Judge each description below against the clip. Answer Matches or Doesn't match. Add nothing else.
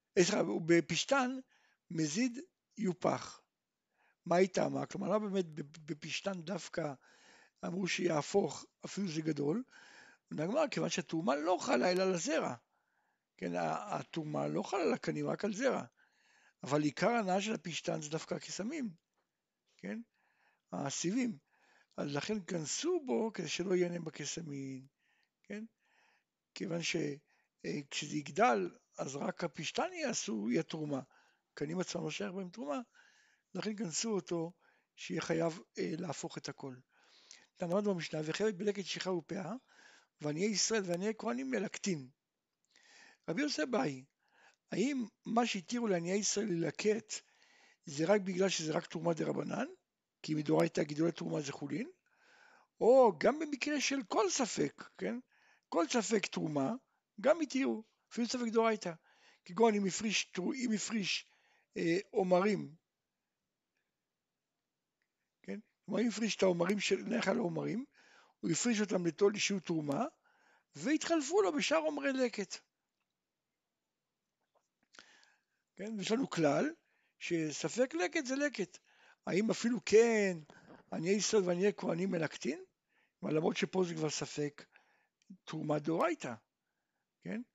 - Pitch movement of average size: Doesn't match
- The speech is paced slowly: Doesn't match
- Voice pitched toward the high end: Matches